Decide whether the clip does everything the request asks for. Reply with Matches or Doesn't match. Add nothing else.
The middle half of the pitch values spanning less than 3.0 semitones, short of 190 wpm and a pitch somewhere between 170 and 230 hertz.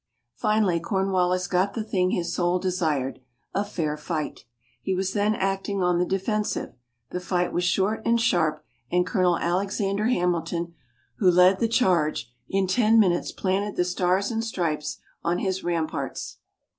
Matches